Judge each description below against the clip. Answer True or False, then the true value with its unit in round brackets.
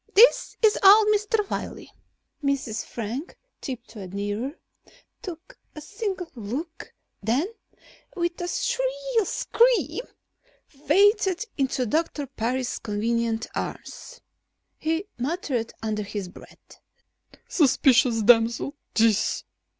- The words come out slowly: True (95 wpm)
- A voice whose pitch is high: True (280 Hz)